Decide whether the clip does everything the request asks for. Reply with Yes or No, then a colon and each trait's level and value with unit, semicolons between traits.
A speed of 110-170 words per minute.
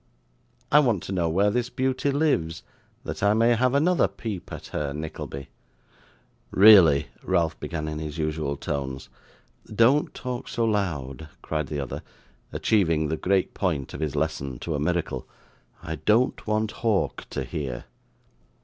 Yes: average, 155 wpm